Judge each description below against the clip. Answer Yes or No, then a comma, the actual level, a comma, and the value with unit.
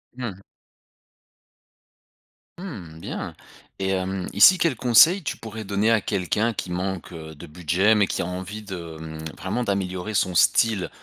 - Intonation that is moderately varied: Yes, average, 3.7 semitones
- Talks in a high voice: No, very low, 95 Hz